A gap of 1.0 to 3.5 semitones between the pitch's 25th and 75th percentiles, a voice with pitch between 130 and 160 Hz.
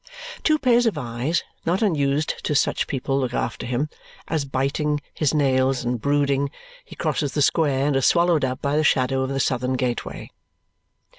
Yes: average, 2.7 semitones; medium, 140 Hz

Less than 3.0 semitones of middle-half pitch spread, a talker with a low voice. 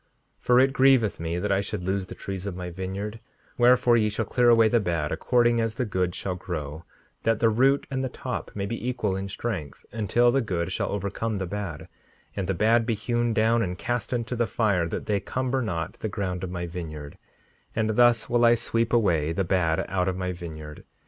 No: average, 4.6 semitones; low, 105 Hz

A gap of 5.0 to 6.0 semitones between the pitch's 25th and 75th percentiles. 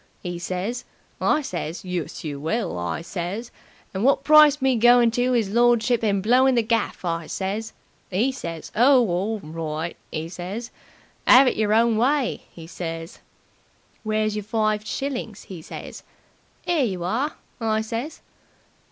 Yes: wide, 5.5 semitones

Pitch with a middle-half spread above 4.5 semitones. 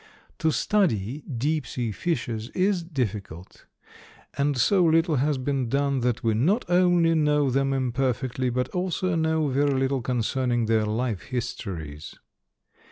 Yes: average, 5.1 semitones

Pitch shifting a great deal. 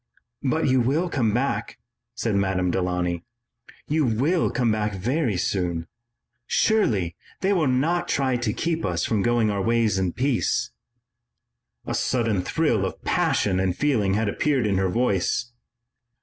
Yes: wide, 6.0 semitones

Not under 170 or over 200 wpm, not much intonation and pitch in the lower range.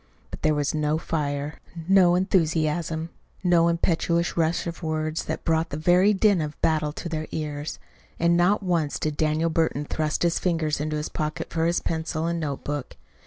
No: average, 175 wpm; narrow, 1.8 semitones; medium, 160 Hz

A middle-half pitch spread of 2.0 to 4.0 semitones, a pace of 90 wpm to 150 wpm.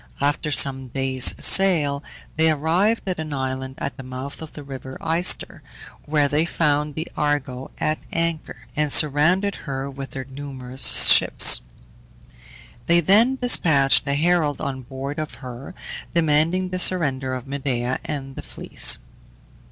Yes: average, 3.4 semitones; average, 145 wpm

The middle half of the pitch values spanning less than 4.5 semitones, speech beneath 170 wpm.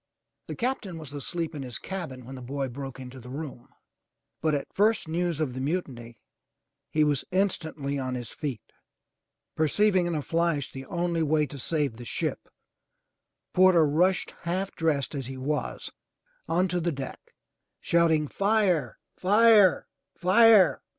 No: average, 5.0 semitones; average, 150 wpm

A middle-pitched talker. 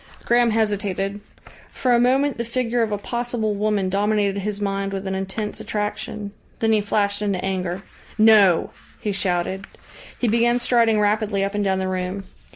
No: high, 205 Hz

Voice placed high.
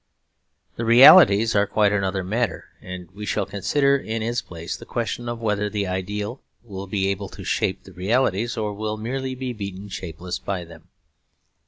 No: low, 105 Hz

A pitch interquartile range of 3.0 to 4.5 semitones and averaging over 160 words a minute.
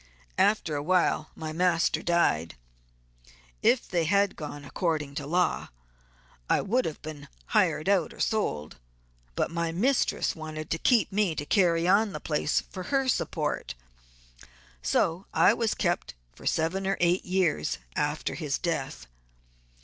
No: average, 4.0 semitones; average, 140 wpm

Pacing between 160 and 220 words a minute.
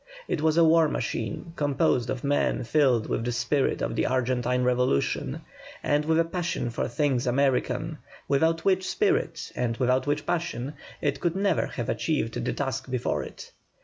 Yes: average, 170 wpm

